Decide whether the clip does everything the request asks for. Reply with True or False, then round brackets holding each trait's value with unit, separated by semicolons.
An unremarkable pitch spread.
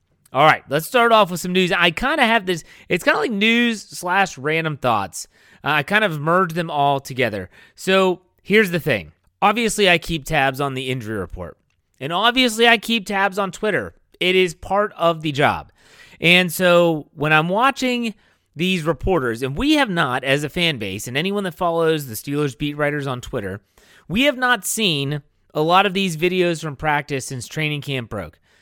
False (5.9 semitones)